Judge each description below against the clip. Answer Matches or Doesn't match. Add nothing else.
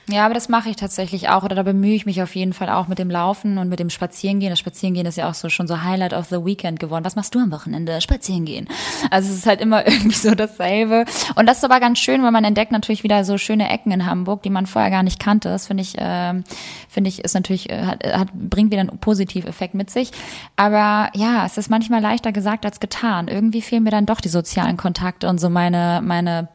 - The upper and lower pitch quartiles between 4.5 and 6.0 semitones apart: Doesn't match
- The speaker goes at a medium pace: Doesn't match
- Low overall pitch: Doesn't match